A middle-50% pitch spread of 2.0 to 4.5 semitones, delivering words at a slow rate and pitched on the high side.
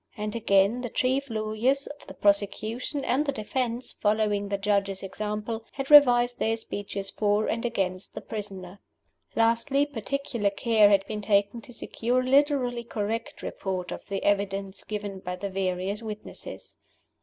No: average, 3.3 semitones; average, 155 wpm; high, 215 Hz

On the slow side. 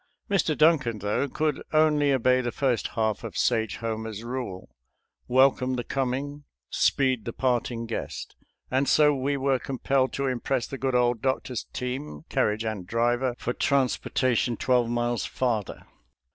No: average, 145 wpm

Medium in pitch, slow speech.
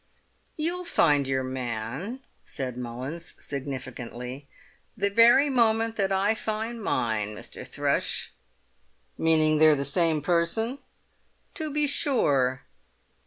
Yes: medium, 160 Hz; slow, 110 wpm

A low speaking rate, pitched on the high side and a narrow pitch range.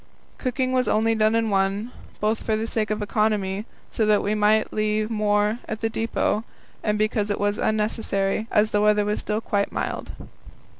No: average, 185 wpm; high, 215 Hz; narrow, 1.0 semitones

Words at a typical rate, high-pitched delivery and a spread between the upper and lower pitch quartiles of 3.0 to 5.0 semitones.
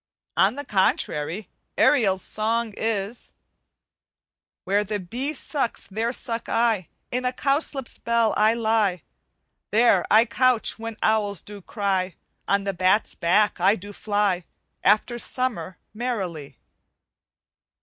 No: slow, 120 wpm; high, 215 Hz; average, 3.3 semitones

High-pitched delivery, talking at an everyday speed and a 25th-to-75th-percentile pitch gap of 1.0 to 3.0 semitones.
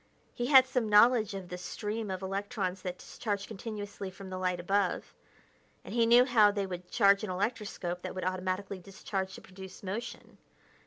Yes: high, 195 Hz; average, 175 wpm; narrow, 2.6 semitones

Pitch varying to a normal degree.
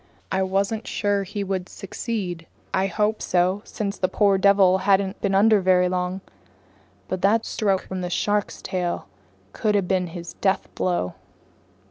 No: narrow, 1.8 semitones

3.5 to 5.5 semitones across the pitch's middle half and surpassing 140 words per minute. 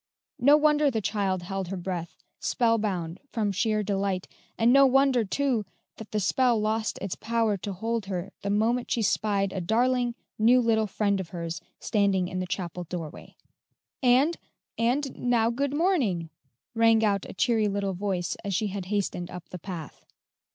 Yes: average, 3.9 semitones; average, 170 wpm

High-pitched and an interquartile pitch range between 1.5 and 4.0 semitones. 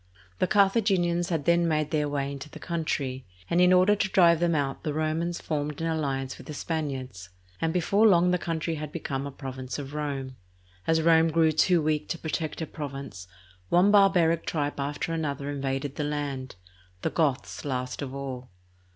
No: medium, 155 Hz; average, 3.4 semitones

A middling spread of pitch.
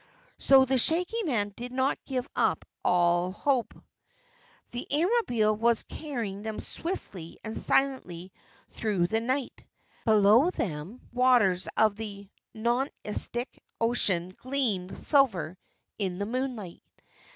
Yes: average, 5.0 semitones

